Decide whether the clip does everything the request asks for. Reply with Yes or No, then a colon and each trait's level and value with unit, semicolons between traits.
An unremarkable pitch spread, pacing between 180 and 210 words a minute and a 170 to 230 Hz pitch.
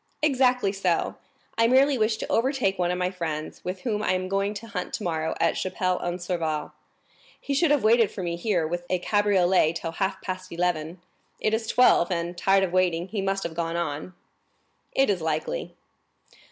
Yes: average, 3.8 semitones; average, 190 wpm; medium, 185 Hz